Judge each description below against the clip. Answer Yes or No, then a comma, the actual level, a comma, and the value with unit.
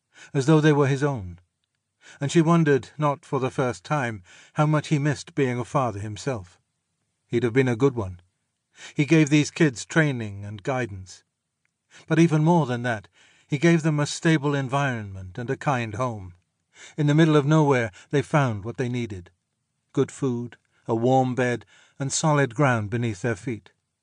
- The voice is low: Yes, low, 130 Hz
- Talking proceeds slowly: No, average, 175 wpm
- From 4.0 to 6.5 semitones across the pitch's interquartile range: Yes, average, 4.5 semitones